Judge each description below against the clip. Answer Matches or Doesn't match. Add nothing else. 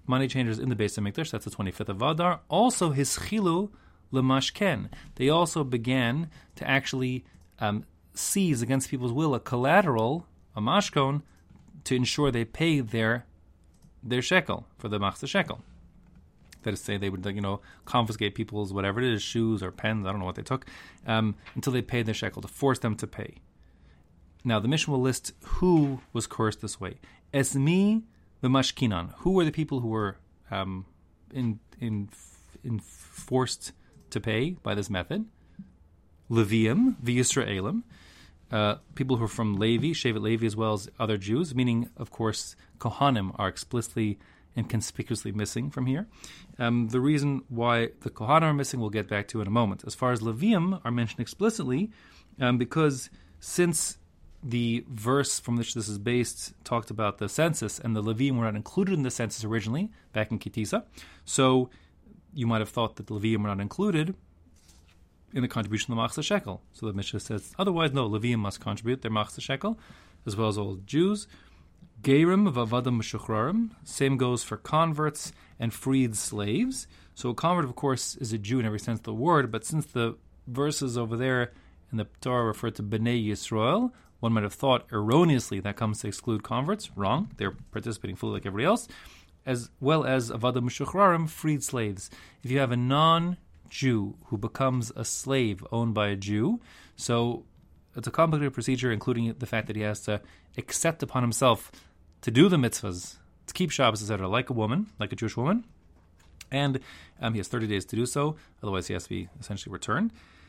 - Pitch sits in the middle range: Doesn't match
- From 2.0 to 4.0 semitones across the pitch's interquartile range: Doesn't match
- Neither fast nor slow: Matches